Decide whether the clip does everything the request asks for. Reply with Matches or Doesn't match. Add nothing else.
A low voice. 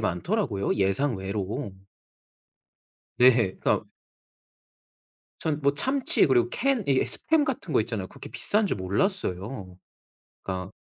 Matches